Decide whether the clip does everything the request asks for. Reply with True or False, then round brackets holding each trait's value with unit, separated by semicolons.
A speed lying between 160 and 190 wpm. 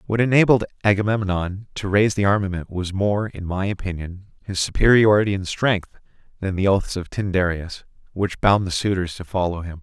True (170 wpm)